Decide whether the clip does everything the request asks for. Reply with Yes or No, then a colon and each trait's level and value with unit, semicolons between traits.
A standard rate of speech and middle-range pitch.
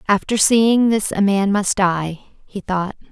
No: average, 175 wpm; high, 200 Hz